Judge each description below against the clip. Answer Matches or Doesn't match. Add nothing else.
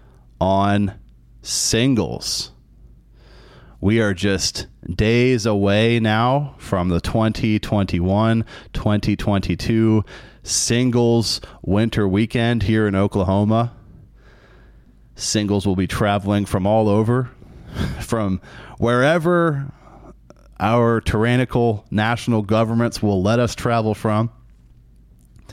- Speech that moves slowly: Matches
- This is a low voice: Matches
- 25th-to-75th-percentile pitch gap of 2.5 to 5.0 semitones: Matches